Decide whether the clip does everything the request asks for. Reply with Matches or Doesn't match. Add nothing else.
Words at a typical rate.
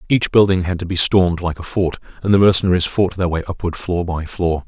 Doesn't match